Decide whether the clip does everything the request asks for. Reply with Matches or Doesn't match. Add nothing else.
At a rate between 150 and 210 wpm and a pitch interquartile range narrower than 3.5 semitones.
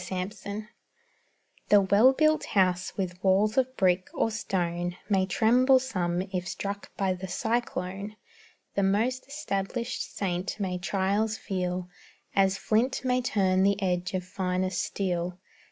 Doesn't match